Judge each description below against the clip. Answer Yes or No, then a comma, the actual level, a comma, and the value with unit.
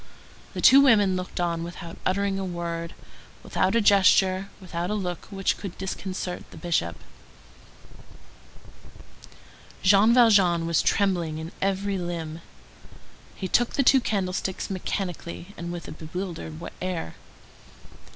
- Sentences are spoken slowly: Yes, slow, 125 wpm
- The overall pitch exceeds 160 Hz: Yes, medium, 185 Hz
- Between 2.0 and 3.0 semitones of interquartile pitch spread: Yes, narrow, 2.6 semitones